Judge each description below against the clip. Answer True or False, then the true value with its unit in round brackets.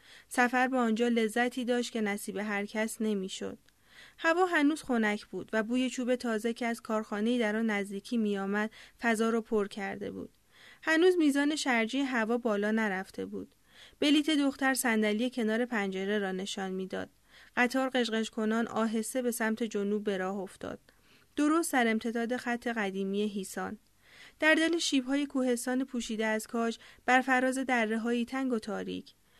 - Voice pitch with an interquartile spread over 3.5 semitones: False (3.2 semitones)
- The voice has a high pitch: True (230 Hz)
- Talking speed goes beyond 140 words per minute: True (150 wpm)